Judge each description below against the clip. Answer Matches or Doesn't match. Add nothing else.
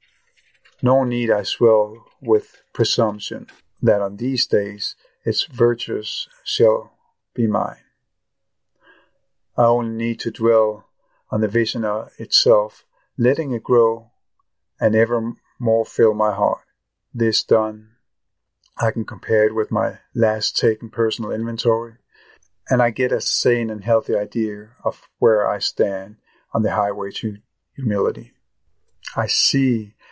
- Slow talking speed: Matches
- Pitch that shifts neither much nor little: Doesn't match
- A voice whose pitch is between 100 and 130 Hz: Matches